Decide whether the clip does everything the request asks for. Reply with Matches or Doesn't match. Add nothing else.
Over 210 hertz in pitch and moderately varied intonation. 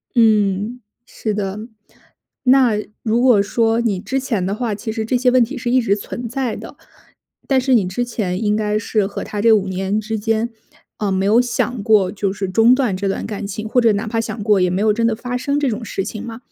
Matches